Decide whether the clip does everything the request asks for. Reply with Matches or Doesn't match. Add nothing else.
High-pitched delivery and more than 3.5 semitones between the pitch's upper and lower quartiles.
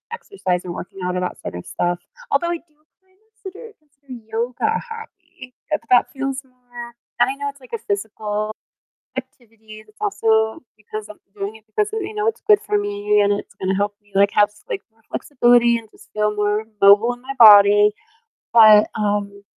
Matches